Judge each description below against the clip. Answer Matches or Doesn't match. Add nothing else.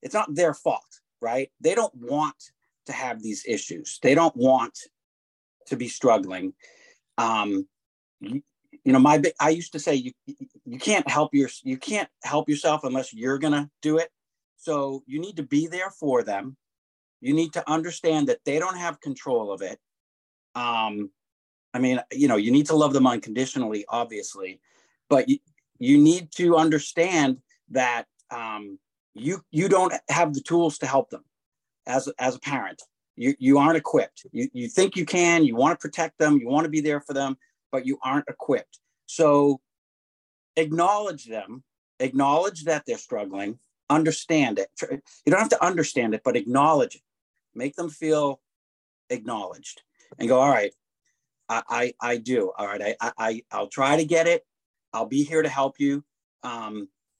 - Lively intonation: Doesn't match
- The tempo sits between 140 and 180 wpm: Matches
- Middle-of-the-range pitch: Matches